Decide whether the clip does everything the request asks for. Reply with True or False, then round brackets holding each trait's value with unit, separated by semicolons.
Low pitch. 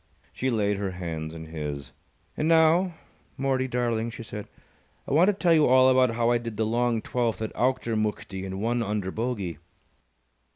True (115 Hz)